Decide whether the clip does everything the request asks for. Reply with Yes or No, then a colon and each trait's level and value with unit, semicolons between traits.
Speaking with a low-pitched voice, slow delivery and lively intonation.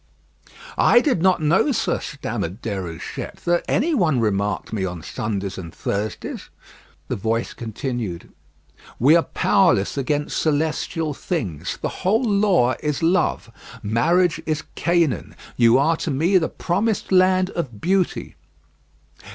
No: medium, 150 Hz; slow, 130 wpm; wide, 8.5 semitones